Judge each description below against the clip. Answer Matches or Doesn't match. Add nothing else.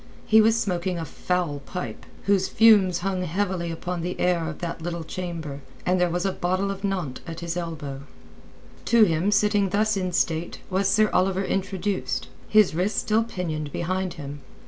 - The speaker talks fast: Doesn't match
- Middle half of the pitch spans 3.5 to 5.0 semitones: Doesn't match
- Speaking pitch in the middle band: Matches